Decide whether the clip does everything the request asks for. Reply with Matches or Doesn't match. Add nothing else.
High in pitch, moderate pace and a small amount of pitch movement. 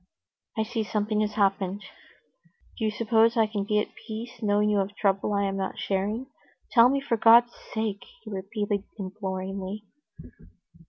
Matches